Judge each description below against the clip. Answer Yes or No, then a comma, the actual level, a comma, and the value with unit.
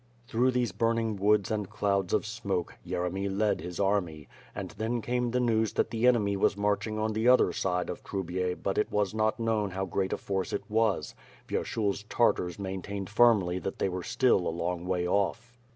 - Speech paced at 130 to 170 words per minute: No, average, 200 wpm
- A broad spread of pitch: No, average, 3.1 semitones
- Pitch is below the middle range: Yes, low, 100 Hz